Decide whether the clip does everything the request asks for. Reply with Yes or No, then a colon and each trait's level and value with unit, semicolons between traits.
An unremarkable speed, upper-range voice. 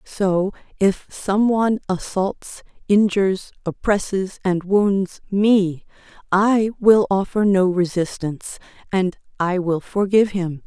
No: slow, 105 wpm; high, 195 Hz